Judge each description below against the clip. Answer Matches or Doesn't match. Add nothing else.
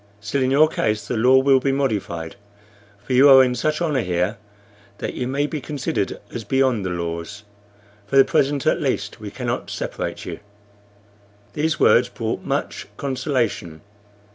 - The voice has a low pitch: Matches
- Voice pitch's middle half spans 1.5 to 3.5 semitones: Doesn't match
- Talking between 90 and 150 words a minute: Doesn't match